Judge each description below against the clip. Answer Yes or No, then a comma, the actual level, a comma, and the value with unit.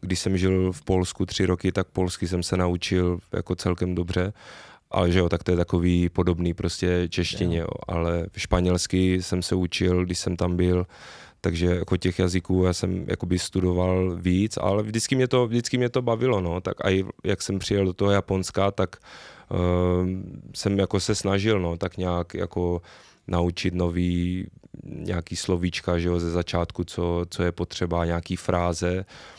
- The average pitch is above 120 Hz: No, very low, 90 Hz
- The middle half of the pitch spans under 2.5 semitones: Yes, narrow, 1.4 semitones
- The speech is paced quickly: Yes, fast, 175 wpm